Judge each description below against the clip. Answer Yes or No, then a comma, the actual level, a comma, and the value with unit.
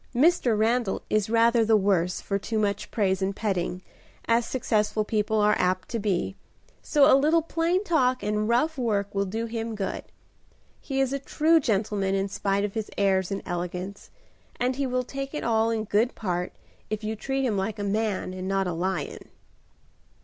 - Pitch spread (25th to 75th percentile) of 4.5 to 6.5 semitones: No, average, 3.9 semitones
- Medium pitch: No, high, 215 Hz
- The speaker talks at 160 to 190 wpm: Yes, average, 185 wpm